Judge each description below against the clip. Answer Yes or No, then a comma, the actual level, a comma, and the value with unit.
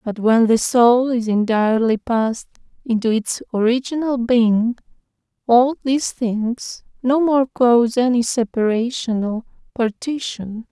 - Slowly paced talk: Yes, slow, 120 wpm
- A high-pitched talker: Yes, high, 235 Hz